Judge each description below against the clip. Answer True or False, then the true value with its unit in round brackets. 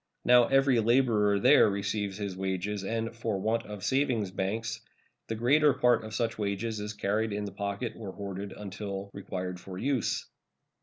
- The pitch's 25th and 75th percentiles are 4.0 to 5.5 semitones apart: False (2.6 semitones)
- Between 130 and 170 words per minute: True (165 wpm)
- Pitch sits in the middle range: False (105 Hz)